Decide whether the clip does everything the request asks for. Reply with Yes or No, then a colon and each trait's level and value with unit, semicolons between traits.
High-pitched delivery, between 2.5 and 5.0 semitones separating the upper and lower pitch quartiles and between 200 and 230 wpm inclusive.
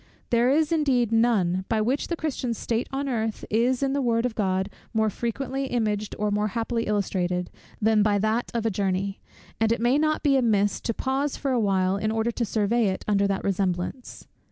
Yes: high, 225 Hz; average, 3.6 semitones; fast, 205 wpm